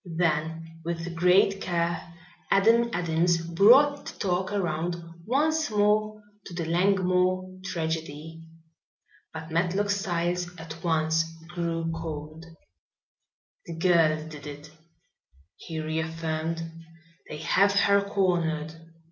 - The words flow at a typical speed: No, slow, 105 wpm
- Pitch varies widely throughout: No, average, 3.0 semitones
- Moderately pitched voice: Yes, medium, 170 Hz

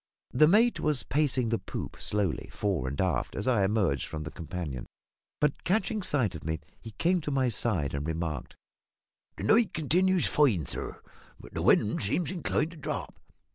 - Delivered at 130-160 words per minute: No, average, 175 wpm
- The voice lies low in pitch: Yes, low, 115 Hz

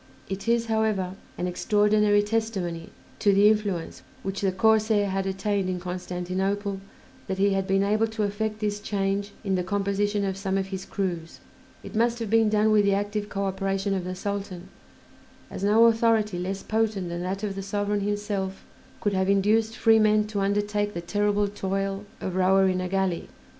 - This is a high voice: Yes, high, 200 Hz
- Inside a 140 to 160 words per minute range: No, average, 180 wpm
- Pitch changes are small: Yes, narrow, 1.6 semitones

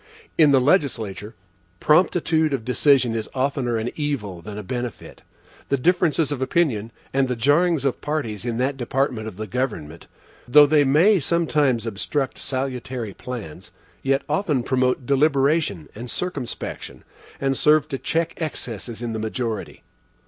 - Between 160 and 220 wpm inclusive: No, average, 145 wpm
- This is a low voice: Yes, low, 130 Hz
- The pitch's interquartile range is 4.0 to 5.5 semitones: Yes, average, 4.4 semitones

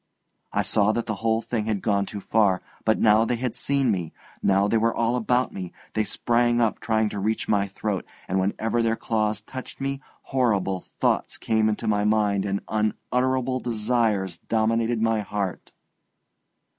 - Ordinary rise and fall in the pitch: No, narrow, 2.3 semitones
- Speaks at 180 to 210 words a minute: No, average, 170 wpm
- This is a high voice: No, low, 110 Hz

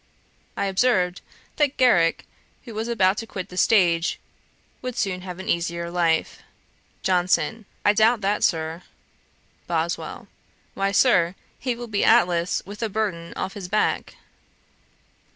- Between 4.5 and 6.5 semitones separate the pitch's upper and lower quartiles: No, average, 4.1 semitones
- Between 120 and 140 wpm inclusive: Yes, slow, 135 wpm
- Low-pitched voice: No, high, 195 Hz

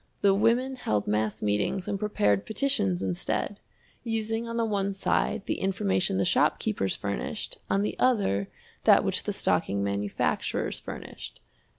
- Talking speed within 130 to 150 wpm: Yes, average, 145 wpm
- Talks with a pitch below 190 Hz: No, high, 195 Hz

